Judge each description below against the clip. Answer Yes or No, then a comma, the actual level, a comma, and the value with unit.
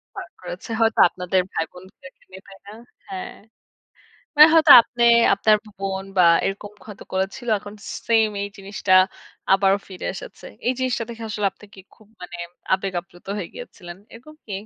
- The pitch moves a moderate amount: Yes, average, 3.0 semitones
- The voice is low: No, high, 200 Hz